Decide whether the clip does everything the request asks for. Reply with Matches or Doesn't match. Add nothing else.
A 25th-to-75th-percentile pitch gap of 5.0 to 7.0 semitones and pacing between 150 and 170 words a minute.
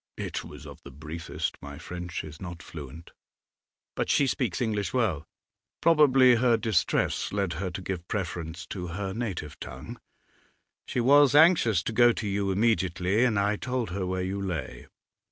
Matches